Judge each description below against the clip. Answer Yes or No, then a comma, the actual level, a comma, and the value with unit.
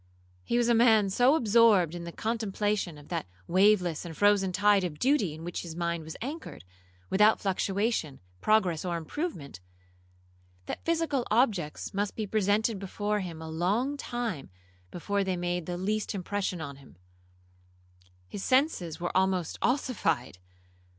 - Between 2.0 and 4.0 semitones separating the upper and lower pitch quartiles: No, average, 5.0 semitones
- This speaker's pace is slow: No, average, 145 wpm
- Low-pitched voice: No, high, 190 Hz